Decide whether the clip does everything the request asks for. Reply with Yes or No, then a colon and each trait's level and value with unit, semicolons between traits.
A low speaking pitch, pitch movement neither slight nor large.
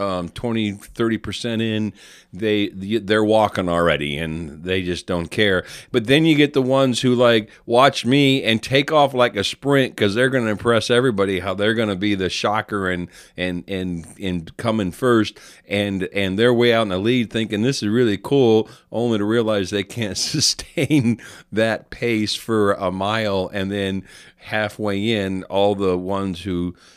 Yes: low, 105 Hz; average, 3.8 semitones